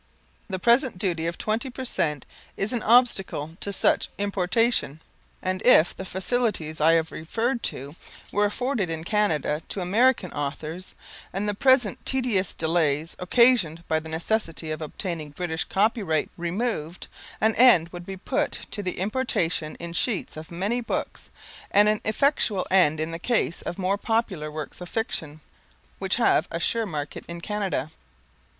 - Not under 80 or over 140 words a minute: No, average, 155 wpm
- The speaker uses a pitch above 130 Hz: Yes, medium, 185 Hz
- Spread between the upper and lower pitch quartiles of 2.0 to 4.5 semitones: No, wide, 5.5 semitones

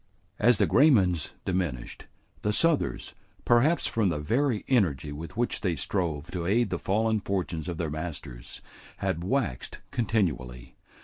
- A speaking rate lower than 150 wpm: Yes, average, 140 wpm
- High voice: No, very low, 90 Hz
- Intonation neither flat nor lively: No, wide, 6.5 semitones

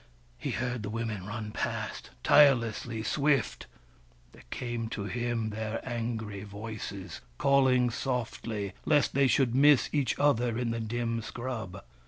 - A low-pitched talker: Yes, low, 115 Hz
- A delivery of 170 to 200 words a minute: No, slow, 135 wpm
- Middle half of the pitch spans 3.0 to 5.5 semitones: No, narrow, 2.5 semitones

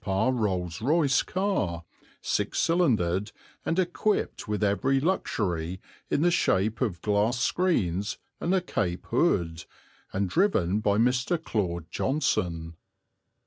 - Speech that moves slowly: Yes, slow, 120 wpm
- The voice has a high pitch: No, low, 105 Hz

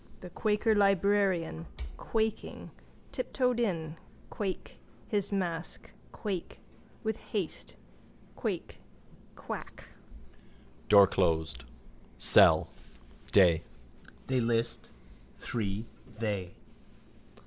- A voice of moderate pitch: Yes, medium, 170 Hz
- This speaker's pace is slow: Yes, slow, 75 wpm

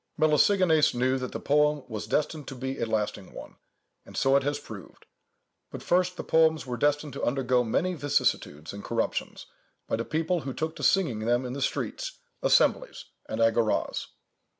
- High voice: No, low, 135 Hz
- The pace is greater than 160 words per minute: Yes, average, 175 wpm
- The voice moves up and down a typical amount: Yes, average, 4.8 semitones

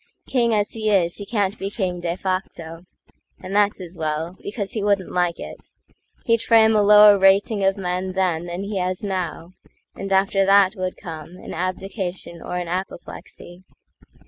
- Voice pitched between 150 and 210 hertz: Yes, high, 190 Hz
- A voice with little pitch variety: Yes, narrow, 2.3 semitones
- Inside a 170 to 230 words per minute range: No, average, 155 wpm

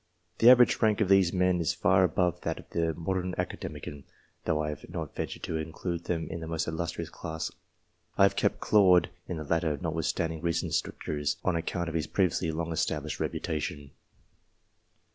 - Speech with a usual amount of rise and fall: No, narrow, 2.2 semitones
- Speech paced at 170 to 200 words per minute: Yes, average, 180 wpm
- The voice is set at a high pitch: No, very low, 85 Hz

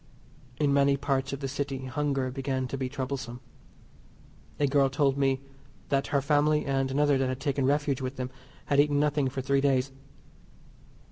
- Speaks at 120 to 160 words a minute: No, average, 175 wpm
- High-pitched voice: No, low, 135 Hz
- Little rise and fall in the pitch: Yes, narrow, 1.3 semitones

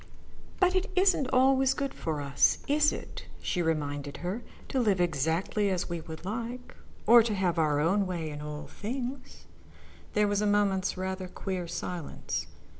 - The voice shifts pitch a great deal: Yes, wide, 6.8 semitones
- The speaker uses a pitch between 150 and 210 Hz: Yes, high, 190 Hz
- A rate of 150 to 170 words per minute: Yes, average, 165 wpm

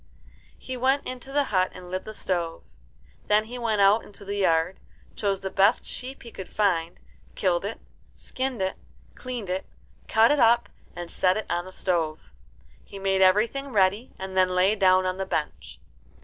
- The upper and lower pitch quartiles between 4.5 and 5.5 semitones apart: No, average, 3.7 semitones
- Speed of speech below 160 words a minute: No, average, 180 wpm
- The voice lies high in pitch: Yes, high, 195 Hz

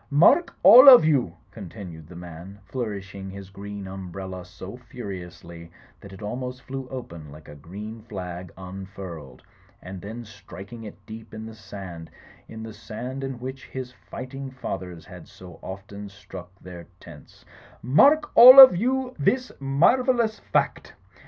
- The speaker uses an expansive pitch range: Yes, wide, 6.0 semitones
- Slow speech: No, average, 145 wpm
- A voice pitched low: Yes, low, 100 Hz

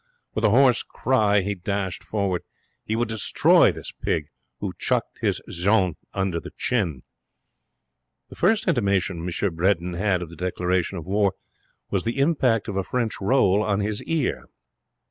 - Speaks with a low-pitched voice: Yes, low, 100 Hz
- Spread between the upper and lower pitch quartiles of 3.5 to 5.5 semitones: Yes, average, 3.8 semitones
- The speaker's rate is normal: Yes, average, 160 wpm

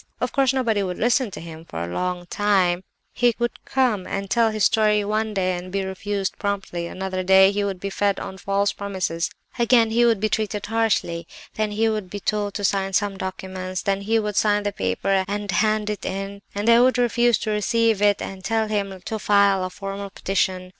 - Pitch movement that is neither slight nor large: No, narrow, 2.3 semitones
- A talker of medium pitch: No, high, 200 Hz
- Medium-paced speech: No, fast, 210 wpm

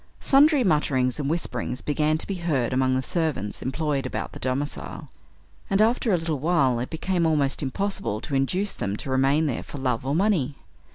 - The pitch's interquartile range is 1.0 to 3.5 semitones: No, average, 4.8 semitones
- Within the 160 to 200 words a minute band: Yes, average, 185 wpm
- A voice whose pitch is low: No, medium, 150 Hz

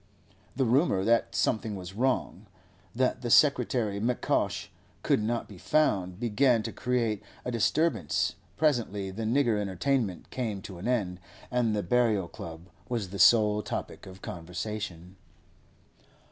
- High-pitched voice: No, low, 110 Hz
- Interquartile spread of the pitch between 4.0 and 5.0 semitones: Yes, average, 4.3 semitones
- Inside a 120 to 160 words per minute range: Yes, slow, 135 wpm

